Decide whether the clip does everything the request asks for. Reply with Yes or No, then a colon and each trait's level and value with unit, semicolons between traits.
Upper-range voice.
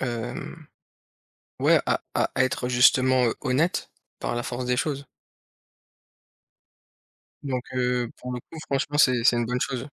No: low, 125 Hz